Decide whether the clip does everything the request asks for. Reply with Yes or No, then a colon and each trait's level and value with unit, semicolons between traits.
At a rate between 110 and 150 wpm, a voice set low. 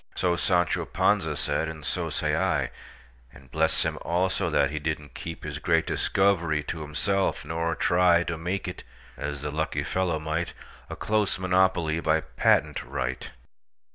Yes: average, 140 wpm; very low, 80 Hz